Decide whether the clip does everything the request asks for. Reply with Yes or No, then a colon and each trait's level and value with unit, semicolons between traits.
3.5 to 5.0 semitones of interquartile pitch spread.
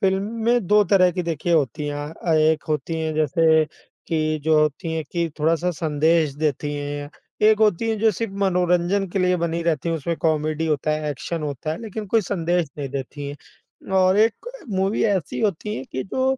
Yes: average, 3.9 semitones